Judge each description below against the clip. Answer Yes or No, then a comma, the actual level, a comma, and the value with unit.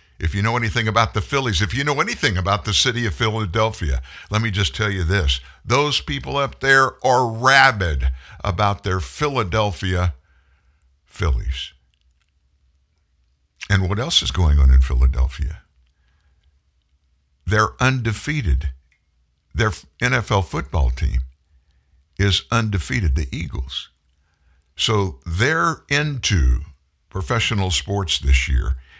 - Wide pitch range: Yes, wide, 7.8 semitones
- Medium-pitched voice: No, very low, 80 Hz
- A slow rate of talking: Yes, slow, 120 wpm